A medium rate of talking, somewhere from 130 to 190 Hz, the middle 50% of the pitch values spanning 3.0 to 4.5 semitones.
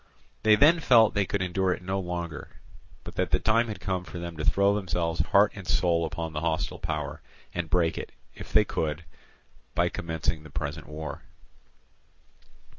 No: average, 185 wpm; very low, 85 Hz; average, 3.6 semitones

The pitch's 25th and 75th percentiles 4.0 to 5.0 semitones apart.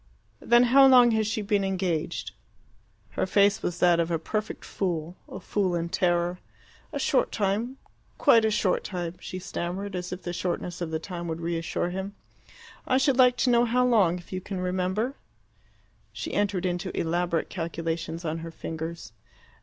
No: average, 3.6 semitones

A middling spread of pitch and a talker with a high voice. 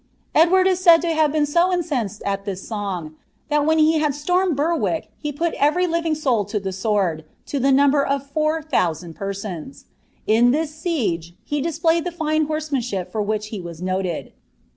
No: wide, 7.9 semitones; very high, 285 Hz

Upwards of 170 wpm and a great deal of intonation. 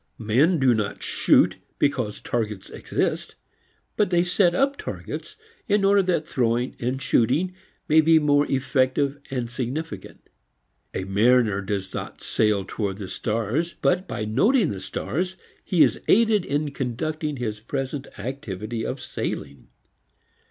No: average, 140 wpm; wide, 6.6 semitones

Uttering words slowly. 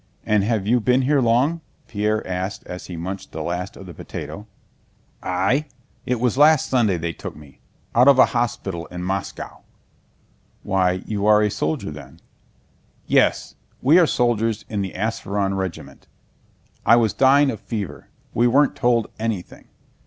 No: average, 160 wpm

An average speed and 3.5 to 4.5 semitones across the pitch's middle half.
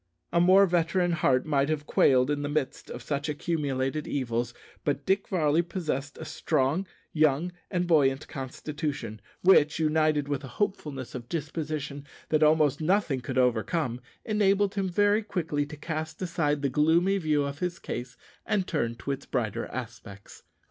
Yes: average, 160 wpm; average, 4.0 semitones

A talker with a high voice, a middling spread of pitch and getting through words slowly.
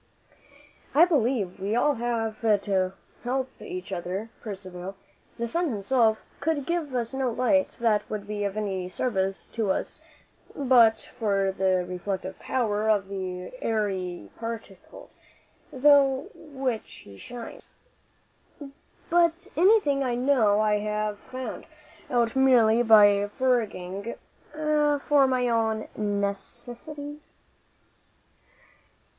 Yes: high, 225 Hz; average, 4.8 semitones; slow, 110 wpm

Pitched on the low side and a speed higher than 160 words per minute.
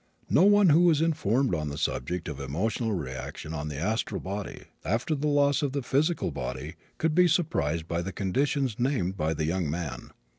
Yes: low, 100 Hz; average, 190 wpm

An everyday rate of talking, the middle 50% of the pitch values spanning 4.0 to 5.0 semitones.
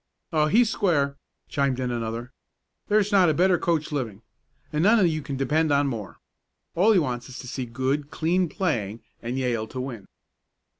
No: average, 180 wpm; wide, 5.5 semitones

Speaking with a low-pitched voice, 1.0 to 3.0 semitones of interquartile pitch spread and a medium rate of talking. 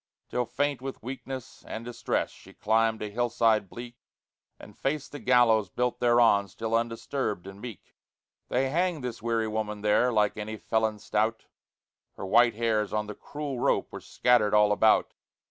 Yes: low, 115 Hz; narrow, 2.6 semitones; average, 165 wpm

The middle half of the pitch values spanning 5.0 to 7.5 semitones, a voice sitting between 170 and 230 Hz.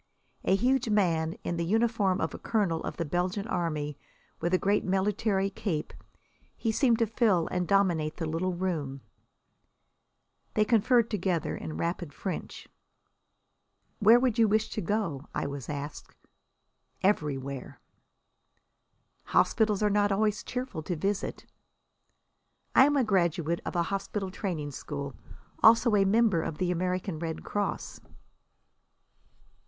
No: average, 4.4 semitones; high, 190 Hz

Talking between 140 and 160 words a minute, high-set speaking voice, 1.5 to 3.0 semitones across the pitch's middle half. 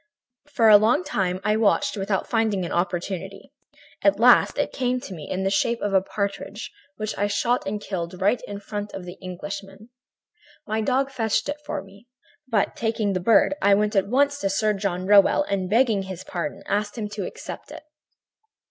No: average, 190 wpm; high, 205 Hz; narrow, 2.5 semitones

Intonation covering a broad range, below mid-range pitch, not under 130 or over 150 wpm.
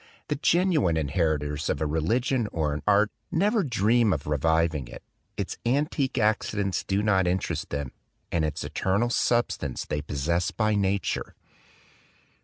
Yes: wide, 7.3 semitones; very low, 95 Hz; average, 145 wpm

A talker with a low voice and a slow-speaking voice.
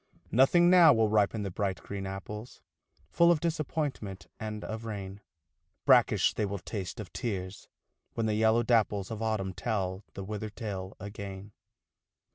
No: low, 105 Hz; average, 150 wpm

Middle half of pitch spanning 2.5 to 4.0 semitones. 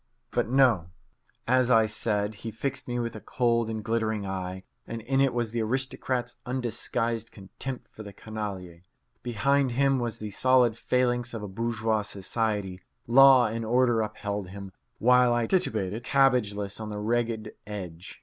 Yes: average, 3.0 semitones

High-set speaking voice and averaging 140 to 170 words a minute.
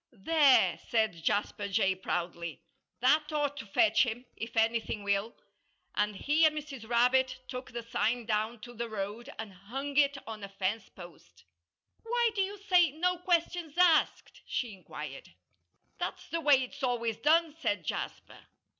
Yes: high, 240 Hz; average, 155 wpm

